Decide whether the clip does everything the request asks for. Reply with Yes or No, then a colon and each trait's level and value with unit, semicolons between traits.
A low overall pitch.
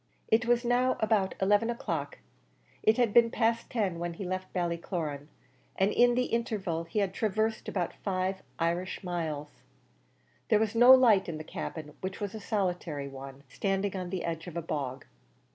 No: high, 190 Hz